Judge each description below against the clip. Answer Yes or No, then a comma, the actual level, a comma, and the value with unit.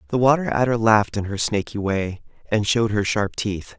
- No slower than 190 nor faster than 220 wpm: Yes, fast, 205 wpm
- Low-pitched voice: Yes, low, 105 Hz